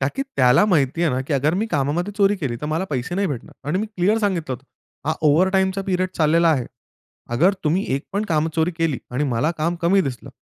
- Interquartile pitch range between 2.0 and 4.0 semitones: No, average, 5.0 semitones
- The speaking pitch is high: No, medium, 165 Hz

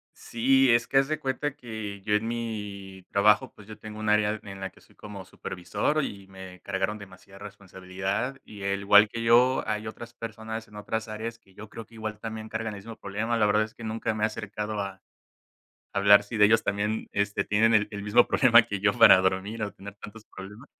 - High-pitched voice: No, low, 105 Hz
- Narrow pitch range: Yes, narrow, 2.0 semitones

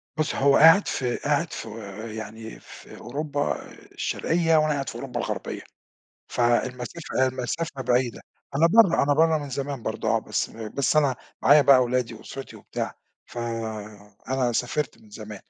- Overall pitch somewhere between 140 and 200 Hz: No, low, 130 Hz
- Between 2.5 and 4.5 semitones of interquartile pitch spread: Yes, average, 4.0 semitones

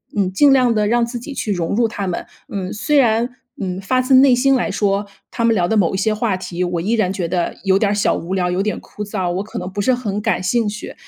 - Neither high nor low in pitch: No, high, 205 Hz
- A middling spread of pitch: Yes, average, 3.9 semitones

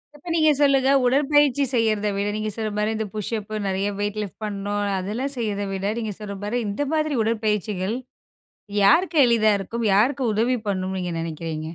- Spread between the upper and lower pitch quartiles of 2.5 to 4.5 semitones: Yes, average, 3.6 semitones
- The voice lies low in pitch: No, high, 215 Hz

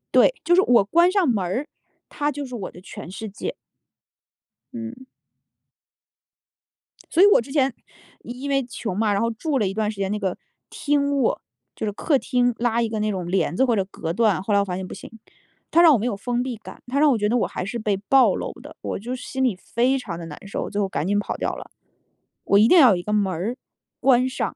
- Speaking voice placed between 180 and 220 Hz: No, high, 230 Hz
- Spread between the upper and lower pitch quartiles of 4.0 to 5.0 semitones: Yes, average, 4.7 semitones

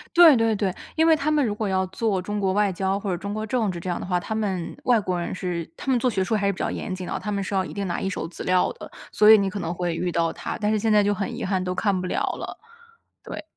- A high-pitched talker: Yes, high, 200 Hz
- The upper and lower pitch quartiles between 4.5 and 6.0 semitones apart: No, average, 2.9 semitones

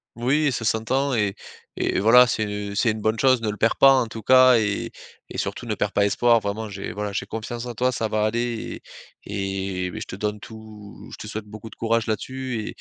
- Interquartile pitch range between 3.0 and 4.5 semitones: No, narrow, 2.6 semitones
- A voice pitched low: Yes, low, 110 Hz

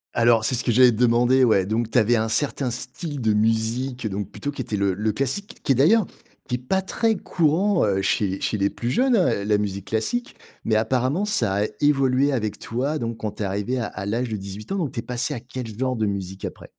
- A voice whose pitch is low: Yes, low, 120 Hz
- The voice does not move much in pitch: No, average, 4.2 semitones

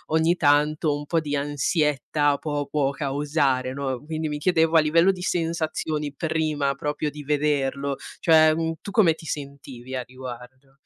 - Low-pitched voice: No, medium, 150 Hz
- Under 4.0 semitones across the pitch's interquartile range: Yes, narrow, 2.4 semitones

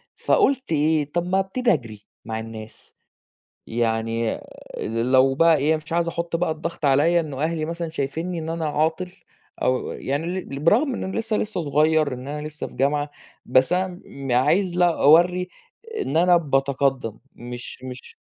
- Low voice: No, medium, 155 Hz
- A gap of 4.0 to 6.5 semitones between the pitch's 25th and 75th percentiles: Yes, average, 4.5 semitones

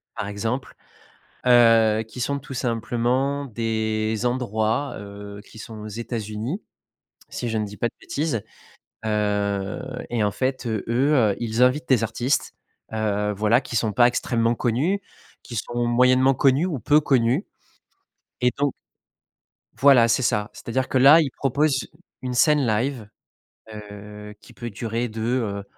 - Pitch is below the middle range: Yes, low, 120 Hz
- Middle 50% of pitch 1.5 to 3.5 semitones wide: Yes, average, 3.2 semitones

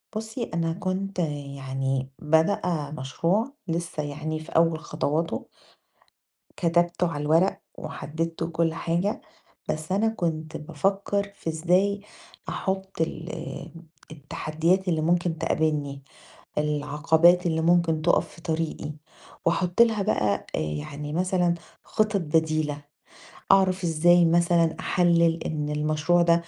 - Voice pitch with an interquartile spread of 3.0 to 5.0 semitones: No, narrow, 2.6 semitones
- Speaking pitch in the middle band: Yes, medium, 165 Hz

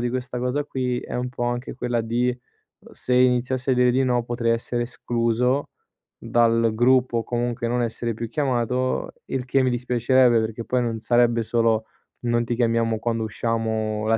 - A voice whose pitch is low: Yes, low, 120 Hz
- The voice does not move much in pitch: Yes, narrow, 1.4 semitones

